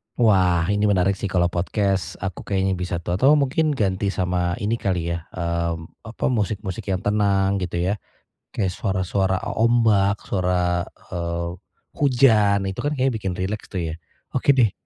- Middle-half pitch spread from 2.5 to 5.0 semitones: Yes, average, 3.0 semitones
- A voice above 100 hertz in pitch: No, very low, 95 Hz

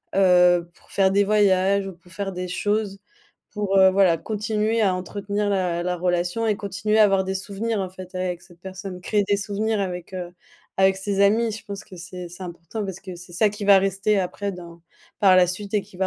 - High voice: Yes, high, 195 Hz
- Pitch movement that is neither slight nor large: No, narrow, 2.1 semitones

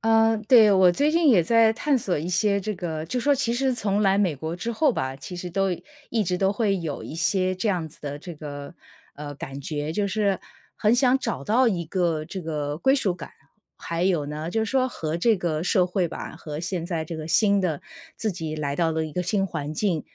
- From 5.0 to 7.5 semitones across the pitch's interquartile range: Yes, average, 5.3 semitones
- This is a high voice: No, medium, 180 Hz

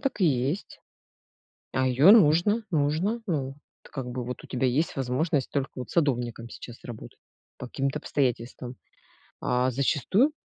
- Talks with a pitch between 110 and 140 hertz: Yes, low, 135 Hz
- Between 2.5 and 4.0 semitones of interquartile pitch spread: No, average, 4.5 semitones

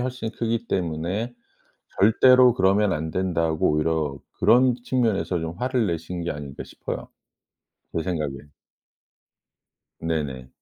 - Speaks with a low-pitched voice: Yes, very low, 90 Hz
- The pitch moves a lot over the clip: Yes, wide, 6.6 semitones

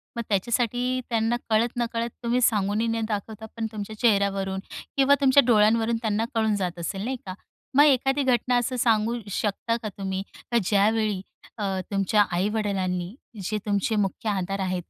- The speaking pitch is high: Yes, high, 220 Hz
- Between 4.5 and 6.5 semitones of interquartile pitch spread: No, average, 3.1 semitones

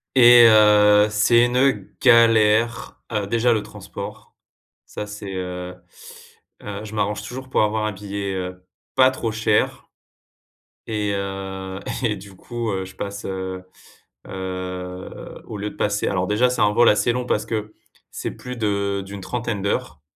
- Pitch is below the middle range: Yes, low, 105 Hz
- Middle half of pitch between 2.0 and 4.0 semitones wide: Yes, average, 3.0 semitones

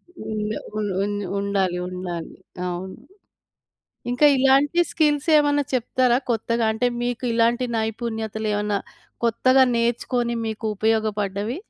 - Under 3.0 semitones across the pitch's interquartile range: No, average, 3.3 semitones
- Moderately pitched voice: No, high, 225 Hz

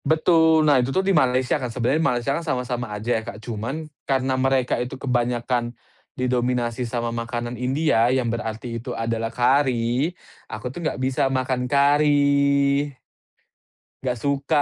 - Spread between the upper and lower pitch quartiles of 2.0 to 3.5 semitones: Yes, average, 2.9 semitones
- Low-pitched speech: Yes, low, 125 Hz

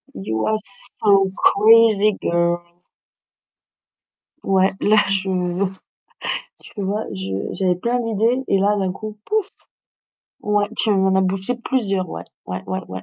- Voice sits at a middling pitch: No, high, 195 Hz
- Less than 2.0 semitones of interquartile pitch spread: No, average, 2.7 semitones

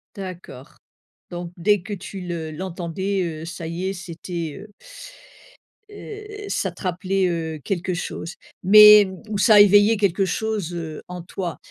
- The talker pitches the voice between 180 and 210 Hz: Yes, medium, 185 Hz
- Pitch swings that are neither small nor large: Yes, average, 3.1 semitones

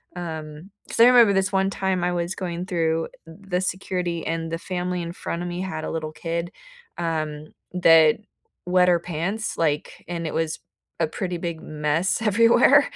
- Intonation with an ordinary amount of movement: No, narrow, 2.2 semitones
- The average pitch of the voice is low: No, medium, 175 Hz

